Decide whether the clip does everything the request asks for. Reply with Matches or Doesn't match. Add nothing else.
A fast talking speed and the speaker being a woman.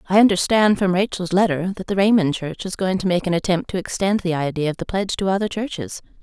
Matches